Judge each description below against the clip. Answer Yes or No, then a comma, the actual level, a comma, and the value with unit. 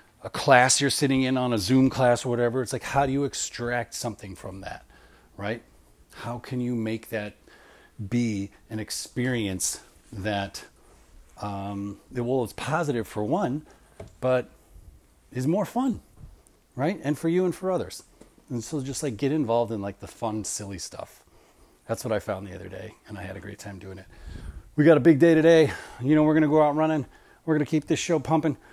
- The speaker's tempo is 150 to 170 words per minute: No, average, 200 wpm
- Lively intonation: Yes, wide, 6.0 semitones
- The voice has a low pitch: Yes, low, 120 Hz